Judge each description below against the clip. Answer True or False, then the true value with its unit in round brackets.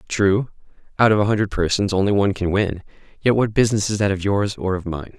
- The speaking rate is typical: False (230 wpm)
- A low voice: True (100 Hz)